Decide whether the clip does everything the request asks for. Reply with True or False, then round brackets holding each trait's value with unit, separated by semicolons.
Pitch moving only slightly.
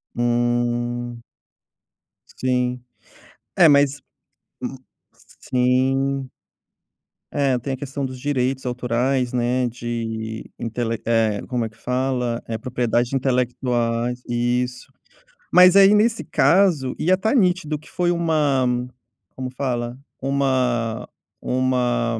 True (2.3 semitones)